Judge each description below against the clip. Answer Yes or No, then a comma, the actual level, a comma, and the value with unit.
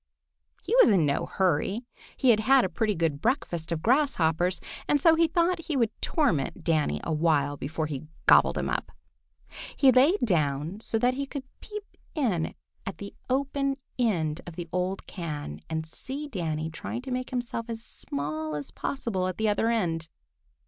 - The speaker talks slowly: No, average, 175 wpm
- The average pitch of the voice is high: Yes, high, 200 Hz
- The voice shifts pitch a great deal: Yes, wide, 8.4 semitones